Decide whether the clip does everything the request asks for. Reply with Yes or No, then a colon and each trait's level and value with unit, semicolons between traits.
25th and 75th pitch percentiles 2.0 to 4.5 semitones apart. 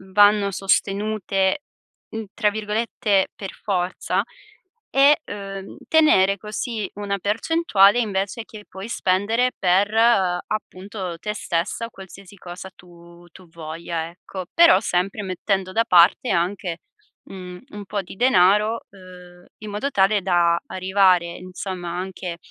Yes: narrow, 2.6 semitones